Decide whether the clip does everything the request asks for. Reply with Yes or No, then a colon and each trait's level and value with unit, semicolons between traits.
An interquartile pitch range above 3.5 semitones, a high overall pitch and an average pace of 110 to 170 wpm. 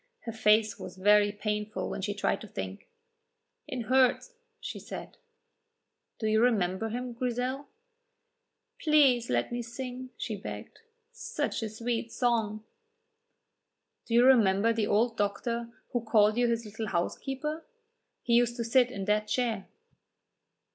No: average, 2.7 semitones; high, 230 Hz; average, 140 wpm